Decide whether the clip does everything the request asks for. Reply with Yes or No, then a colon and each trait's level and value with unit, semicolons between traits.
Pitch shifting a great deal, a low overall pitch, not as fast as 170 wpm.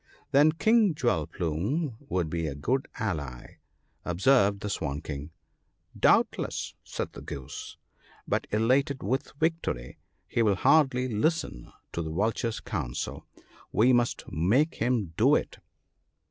Yes: wide, 8.7 semitones; low, 110 Hz; average, 140 wpm